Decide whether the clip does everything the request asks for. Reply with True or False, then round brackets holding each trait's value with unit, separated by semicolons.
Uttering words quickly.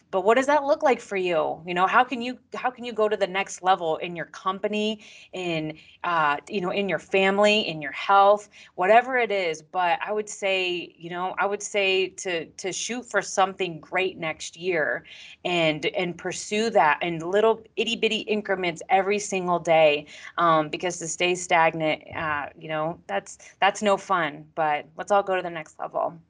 False (195 wpm)